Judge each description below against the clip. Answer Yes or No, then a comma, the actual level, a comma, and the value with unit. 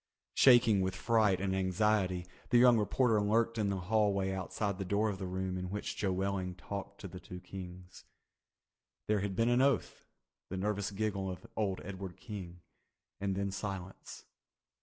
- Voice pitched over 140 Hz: No, low, 100 Hz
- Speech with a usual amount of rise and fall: No, narrow, 2.2 semitones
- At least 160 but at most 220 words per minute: Yes, average, 170 wpm